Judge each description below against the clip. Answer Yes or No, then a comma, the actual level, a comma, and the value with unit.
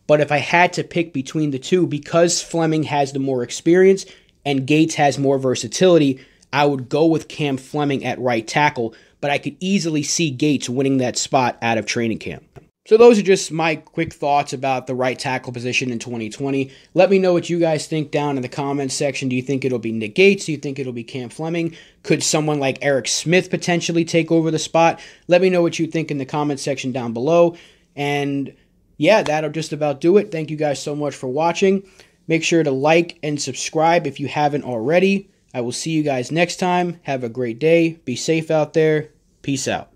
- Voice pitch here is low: No, medium, 150 Hz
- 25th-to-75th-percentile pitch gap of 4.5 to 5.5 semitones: No, average, 3.6 semitones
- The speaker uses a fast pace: Yes, fast, 220 wpm